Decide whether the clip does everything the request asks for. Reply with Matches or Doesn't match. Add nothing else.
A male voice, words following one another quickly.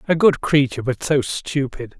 Doesn't match